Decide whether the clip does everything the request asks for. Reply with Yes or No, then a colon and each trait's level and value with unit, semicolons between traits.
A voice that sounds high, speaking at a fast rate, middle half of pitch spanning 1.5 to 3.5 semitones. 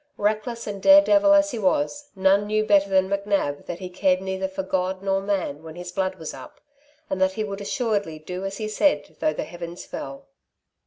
Yes: high, 195 Hz; fast, 210 wpm; average, 2.8 semitones